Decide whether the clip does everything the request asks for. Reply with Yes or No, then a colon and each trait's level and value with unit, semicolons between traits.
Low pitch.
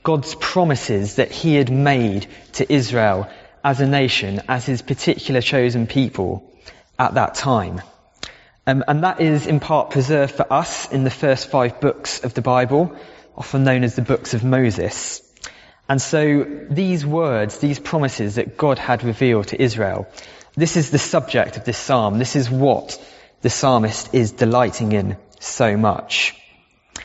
Yes: low, 130 Hz